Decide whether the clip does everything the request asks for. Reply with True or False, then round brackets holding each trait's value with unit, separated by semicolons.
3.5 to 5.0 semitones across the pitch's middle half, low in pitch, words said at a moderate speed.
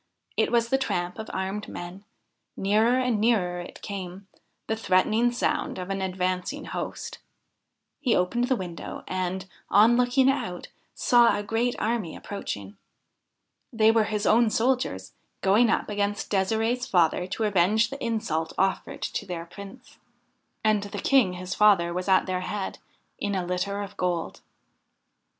False (3.9 semitones; 205 Hz; 150 wpm)